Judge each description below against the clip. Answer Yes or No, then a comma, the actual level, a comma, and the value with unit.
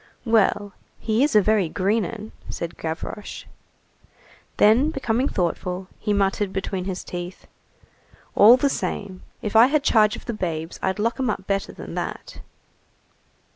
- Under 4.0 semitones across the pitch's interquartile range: Yes, average, 3.3 semitones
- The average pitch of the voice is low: No, high, 205 Hz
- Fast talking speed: No, average, 150 wpm